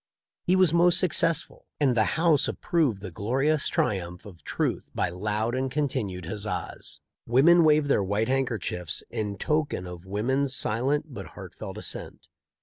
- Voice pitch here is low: Yes, low, 125 Hz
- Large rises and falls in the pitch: Yes, wide, 7.0 semitones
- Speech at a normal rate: Yes, average, 150 wpm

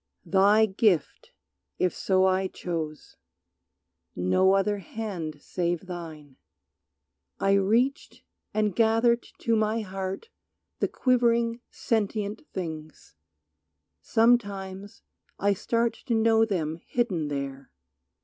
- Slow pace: Yes, slow, 100 wpm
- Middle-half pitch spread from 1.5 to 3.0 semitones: No, average, 4.4 semitones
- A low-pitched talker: No, high, 195 Hz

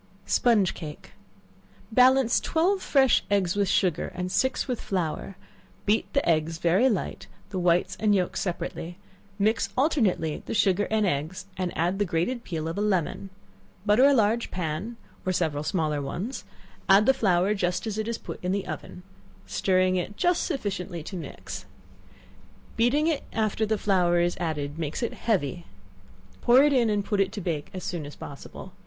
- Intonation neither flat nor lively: Yes, average, 4.5 semitones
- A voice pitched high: Yes, high, 195 Hz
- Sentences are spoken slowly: No, average, 175 wpm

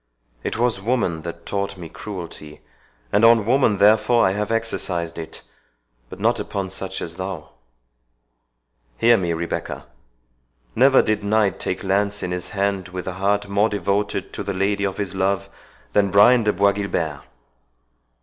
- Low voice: Yes, low, 100 Hz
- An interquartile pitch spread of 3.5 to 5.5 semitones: No, average, 2.8 semitones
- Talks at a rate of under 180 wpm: Yes, average, 155 wpm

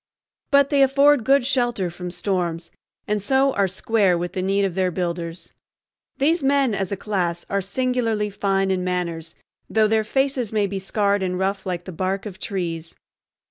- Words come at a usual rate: Yes, average, 180 wpm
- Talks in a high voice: Yes, high, 195 Hz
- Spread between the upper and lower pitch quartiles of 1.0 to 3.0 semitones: No, average, 4.6 semitones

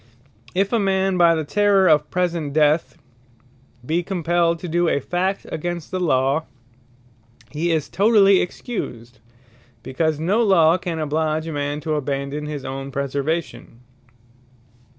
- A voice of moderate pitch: Yes, medium, 160 Hz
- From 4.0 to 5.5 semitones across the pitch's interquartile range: No, average, 3.6 semitones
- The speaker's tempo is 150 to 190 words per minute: No, slow, 135 wpm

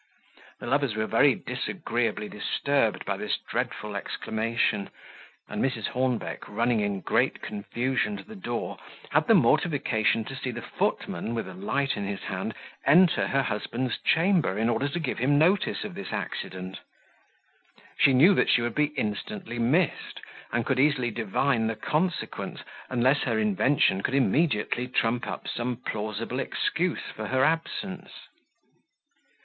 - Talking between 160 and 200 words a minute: No, average, 150 wpm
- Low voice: Yes, low, 125 Hz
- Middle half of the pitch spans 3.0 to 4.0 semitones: No, average, 4.7 semitones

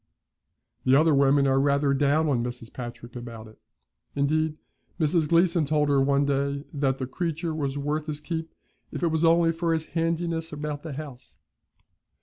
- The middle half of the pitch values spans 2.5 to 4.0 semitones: Yes, average, 2.8 semitones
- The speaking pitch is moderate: Yes, medium, 145 Hz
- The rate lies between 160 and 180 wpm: Yes, average, 170 wpm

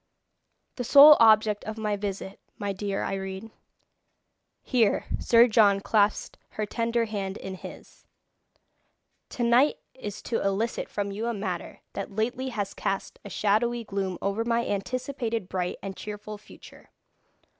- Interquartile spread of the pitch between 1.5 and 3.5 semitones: Yes, average, 2.8 semitones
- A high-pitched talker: Yes, high, 210 Hz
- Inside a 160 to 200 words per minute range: No, slow, 135 wpm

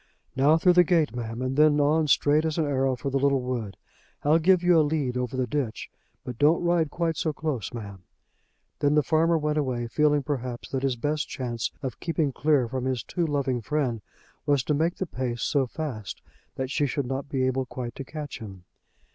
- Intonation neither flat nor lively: Yes, average, 3.5 semitones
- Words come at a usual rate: No, fast, 210 wpm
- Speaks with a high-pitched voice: No, medium, 140 Hz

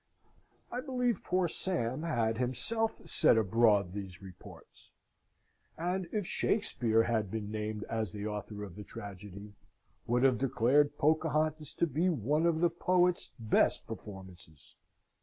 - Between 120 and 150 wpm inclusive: Yes, slow, 135 wpm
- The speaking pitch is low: Yes, low, 120 Hz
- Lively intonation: Yes, wide, 8.1 semitones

